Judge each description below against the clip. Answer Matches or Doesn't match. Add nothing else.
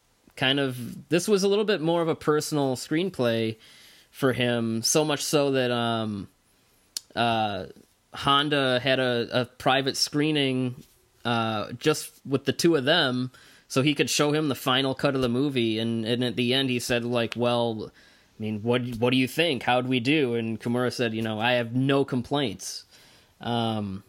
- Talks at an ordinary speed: Matches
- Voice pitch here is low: Matches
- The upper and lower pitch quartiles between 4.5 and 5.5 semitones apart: Doesn't match